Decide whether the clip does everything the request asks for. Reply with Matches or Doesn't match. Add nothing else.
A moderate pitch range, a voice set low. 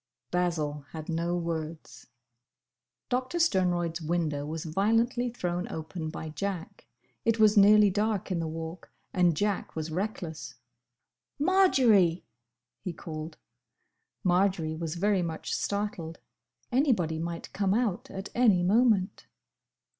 Doesn't match